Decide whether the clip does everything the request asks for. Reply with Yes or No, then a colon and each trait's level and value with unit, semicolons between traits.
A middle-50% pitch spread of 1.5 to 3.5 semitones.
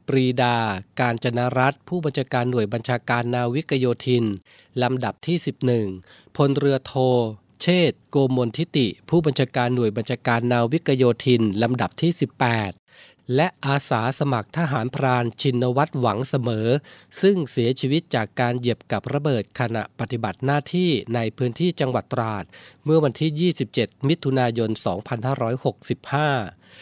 Yes: average, 3.0 semitones